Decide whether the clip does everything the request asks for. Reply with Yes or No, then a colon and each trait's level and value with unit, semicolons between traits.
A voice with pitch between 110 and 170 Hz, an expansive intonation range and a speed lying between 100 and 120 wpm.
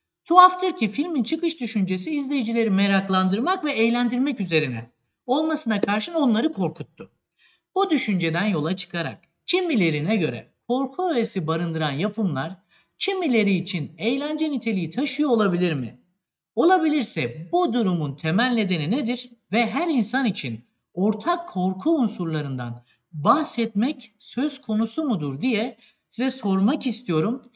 No: high, 225 Hz; wide, 7.1 semitones; average, 115 wpm